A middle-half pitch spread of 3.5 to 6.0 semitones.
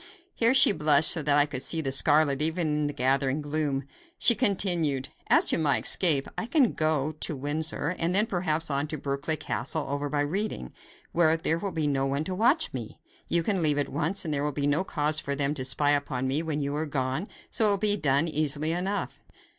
No: average, 2.9 semitones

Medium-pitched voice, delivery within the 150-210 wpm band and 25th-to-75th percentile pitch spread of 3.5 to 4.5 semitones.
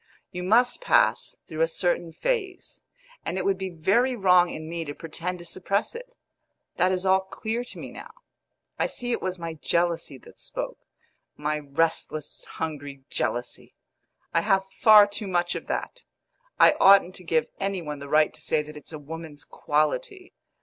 Yes: medium, 175 Hz; average, 175 wpm; average, 4.0 semitones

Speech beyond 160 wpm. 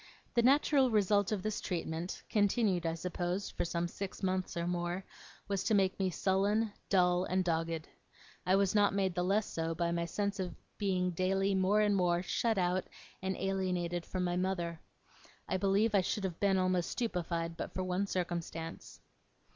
Yes: average, 180 wpm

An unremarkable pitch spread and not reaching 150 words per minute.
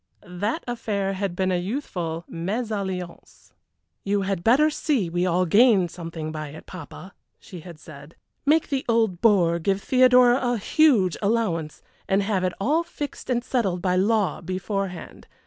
No: average, 4.9 semitones; average, 155 wpm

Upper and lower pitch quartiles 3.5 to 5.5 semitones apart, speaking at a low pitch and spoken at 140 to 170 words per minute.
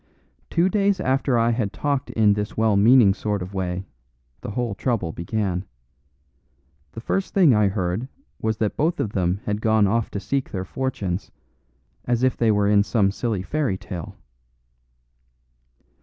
Yes: average, 4.2 semitones; low, 110 Hz; average, 160 wpm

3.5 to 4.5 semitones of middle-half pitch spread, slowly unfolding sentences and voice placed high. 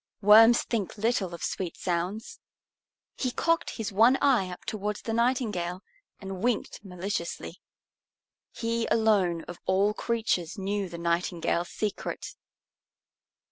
Yes: average, 4.1 semitones; slow, 120 wpm; high, 205 Hz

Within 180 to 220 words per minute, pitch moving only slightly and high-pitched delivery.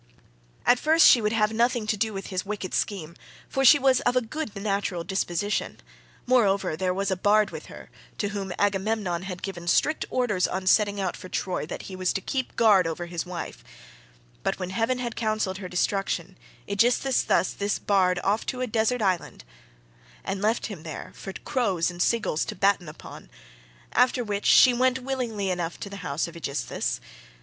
No: average, 185 wpm; average, 3.8 semitones; high, 200 Hz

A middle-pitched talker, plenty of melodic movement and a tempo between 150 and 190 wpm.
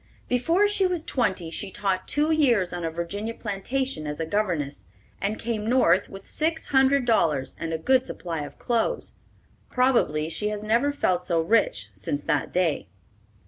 No: high, 210 Hz; wide, 7.8 semitones; average, 170 wpm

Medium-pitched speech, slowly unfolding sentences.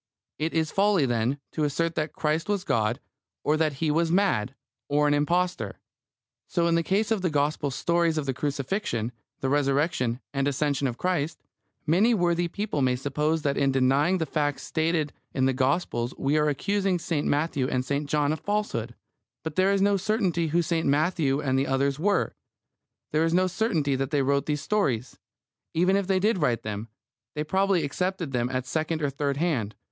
No: medium, 150 Hz; average, 190 wpm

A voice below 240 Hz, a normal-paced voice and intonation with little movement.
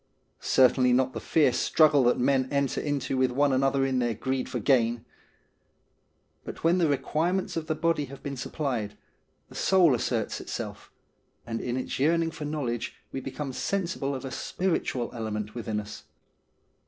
No: low, 135 Hz; average, 165 wpm; average, 3.6 semitones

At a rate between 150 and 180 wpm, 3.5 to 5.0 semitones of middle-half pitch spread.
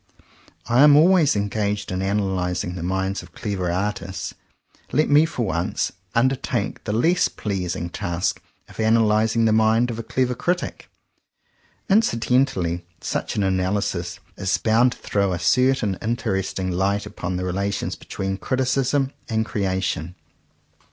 No: average, 140 wpm; average, 4.7 semitones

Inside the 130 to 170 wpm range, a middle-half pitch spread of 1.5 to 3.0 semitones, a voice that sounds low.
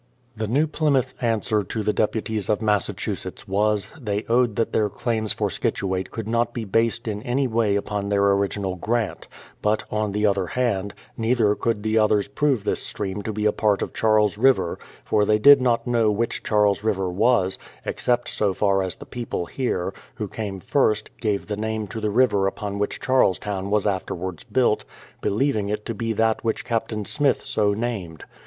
No: average, 190 wpm; narrow, 2.4 semitones; low, 105 Hz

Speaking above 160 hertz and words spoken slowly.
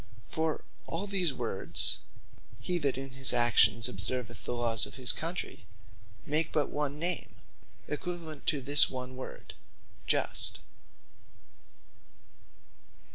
No: low, 135 Hz; slow, 115 wpm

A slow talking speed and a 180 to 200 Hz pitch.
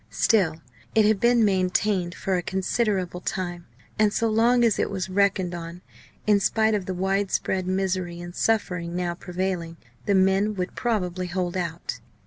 No: average, 165 wpm; high, 190 Hz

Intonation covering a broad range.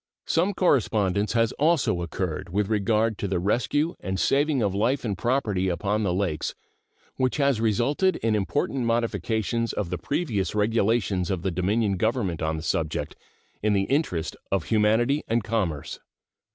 No: average, 3.9 semitones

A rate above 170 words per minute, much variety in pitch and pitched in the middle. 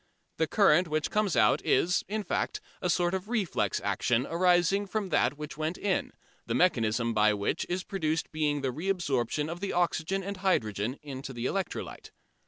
Yes: average, 180 wpm; wide, 6.1 semitones; medium, 165 Hz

